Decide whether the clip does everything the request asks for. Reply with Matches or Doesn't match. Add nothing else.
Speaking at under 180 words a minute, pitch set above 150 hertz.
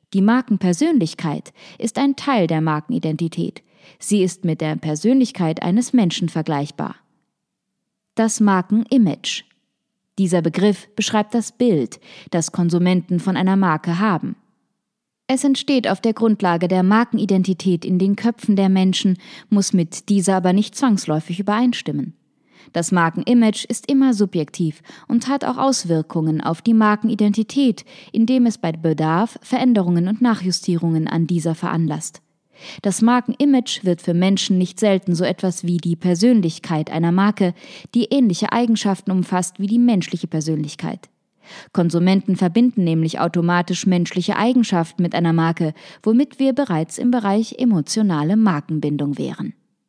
Matches